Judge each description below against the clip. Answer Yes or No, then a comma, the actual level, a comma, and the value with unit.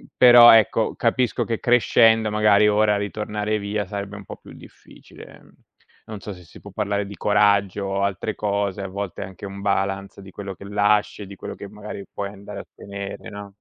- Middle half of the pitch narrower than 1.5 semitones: Yes, narrow, 1.1 semitones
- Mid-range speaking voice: No, low, 100 Hz